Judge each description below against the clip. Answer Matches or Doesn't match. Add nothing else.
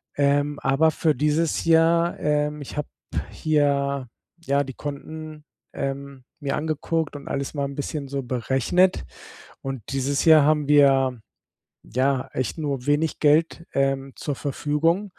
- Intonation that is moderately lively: Doesn't match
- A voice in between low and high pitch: Matches